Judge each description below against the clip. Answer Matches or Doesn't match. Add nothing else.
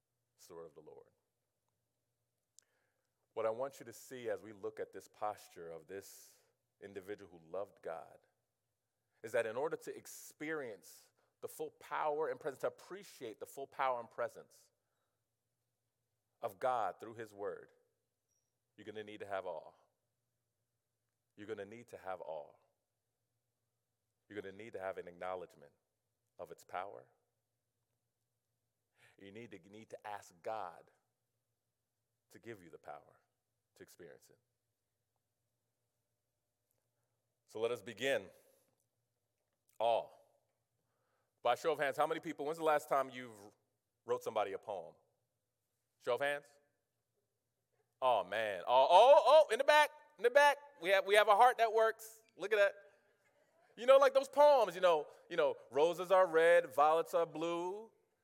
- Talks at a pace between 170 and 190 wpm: Doesn't match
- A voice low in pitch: Matches